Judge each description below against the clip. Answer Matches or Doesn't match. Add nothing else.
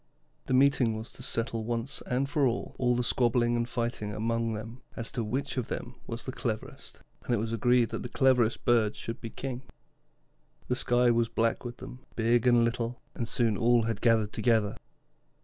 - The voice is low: Matches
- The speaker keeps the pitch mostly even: Matches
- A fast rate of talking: Doesn't match